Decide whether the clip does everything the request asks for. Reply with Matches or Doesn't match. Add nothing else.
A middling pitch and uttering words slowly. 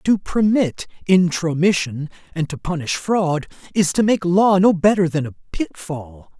Doesn't match